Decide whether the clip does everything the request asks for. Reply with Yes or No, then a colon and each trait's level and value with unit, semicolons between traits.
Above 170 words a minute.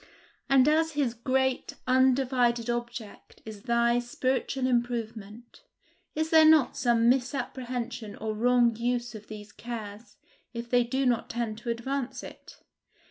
No: slow, 135 wpm